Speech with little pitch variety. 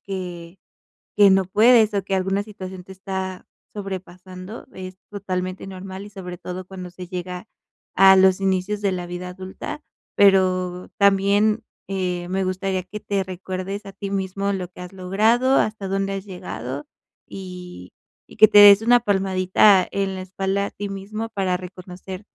Yes: narrow, 1.5 semitones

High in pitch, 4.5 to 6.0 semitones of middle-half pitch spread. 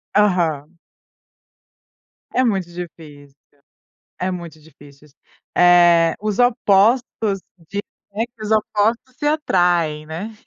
No: medium, 180 Hz; average, 4.9 semitones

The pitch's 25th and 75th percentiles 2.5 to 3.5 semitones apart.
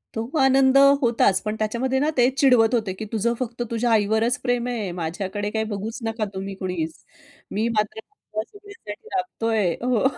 Yes: average, 3.1 semitones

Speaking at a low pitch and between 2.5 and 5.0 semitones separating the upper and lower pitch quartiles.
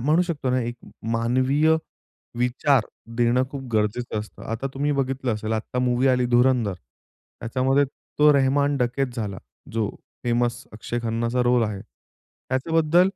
Yes: low, 125 Hz; average, 2.8 semitones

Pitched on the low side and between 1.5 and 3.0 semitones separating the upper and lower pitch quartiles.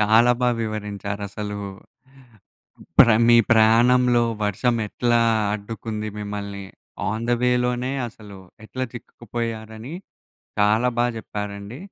Yes: low, 110 Hz; narrow, 2.6 semitones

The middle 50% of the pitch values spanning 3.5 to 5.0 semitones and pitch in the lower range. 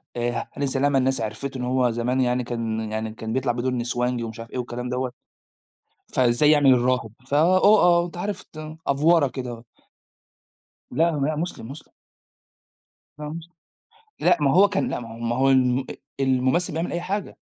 Yes: average, 4.3 semitones; low, 130 Hz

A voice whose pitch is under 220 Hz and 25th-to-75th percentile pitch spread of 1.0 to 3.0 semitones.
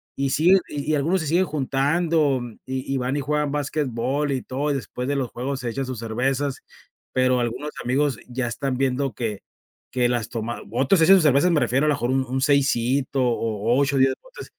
Yes: low, 135 Hz; average, 2.7 semitones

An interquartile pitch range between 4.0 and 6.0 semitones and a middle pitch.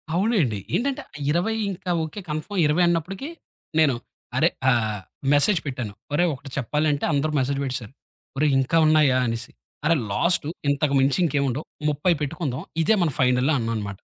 Yes: average, 4.8 semitones; medium, 145 Hz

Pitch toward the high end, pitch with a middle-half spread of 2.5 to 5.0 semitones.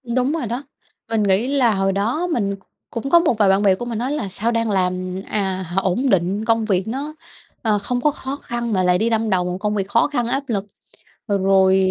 Yes: high, 215 Hz; average, 4.1 semitones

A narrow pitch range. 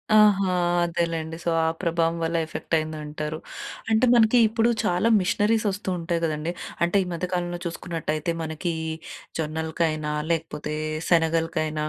Yes: narrow, 2.3 semitones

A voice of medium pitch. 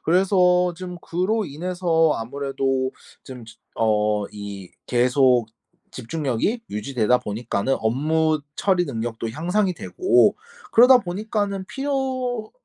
Yes: medium, 160 Hz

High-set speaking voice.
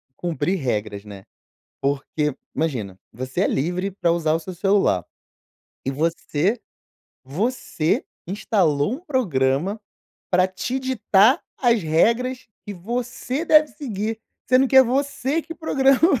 Yes: high, 195 Hz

